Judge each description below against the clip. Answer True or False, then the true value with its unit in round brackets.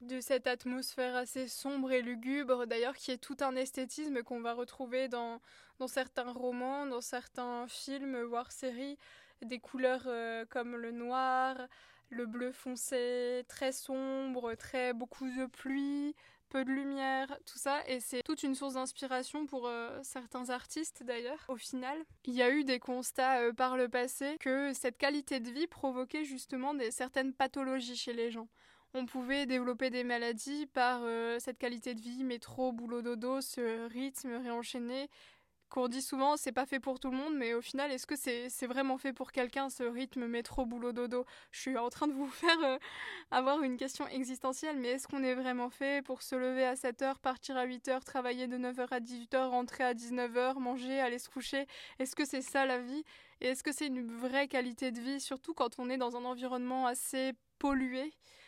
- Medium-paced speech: True (195 wpm)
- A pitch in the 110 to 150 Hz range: False (255 Hz)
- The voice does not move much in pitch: True (1.6 semitones)